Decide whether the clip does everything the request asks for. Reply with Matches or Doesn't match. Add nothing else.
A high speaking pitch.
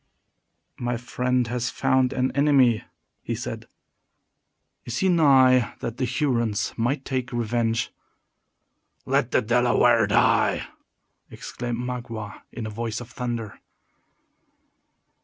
Doesn't match